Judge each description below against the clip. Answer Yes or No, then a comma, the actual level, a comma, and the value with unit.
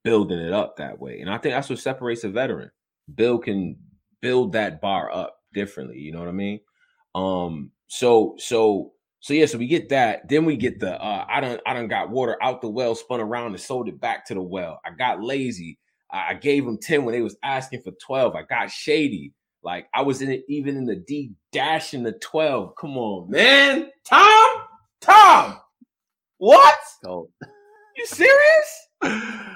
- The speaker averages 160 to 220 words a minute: Yes, average, 195 wpm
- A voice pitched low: Yes, low, 130 Hz